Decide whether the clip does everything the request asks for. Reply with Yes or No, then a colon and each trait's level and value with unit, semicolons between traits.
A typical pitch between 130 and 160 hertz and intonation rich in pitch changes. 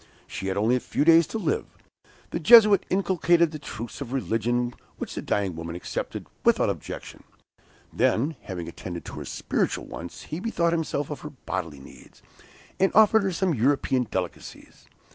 Yes: medium, 140 Hz; wide, 9.0 semitones